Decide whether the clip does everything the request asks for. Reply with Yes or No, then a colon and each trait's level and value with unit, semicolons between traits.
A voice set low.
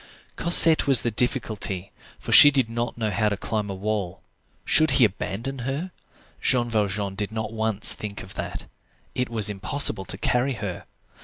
Yes: low, 110 Hz